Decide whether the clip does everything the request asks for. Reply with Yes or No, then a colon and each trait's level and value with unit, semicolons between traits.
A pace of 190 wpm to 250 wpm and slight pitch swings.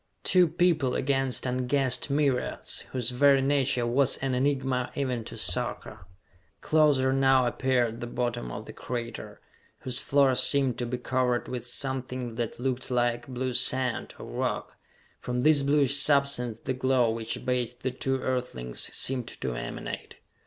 No: average, 150 wpm; narrow, 1.8 semitones